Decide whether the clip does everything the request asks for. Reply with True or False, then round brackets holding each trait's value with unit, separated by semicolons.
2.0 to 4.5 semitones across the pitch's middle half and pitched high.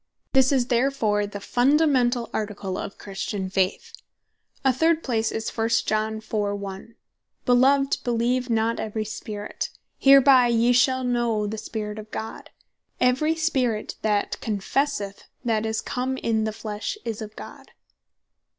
True (3.3 semitones; 230 Hz)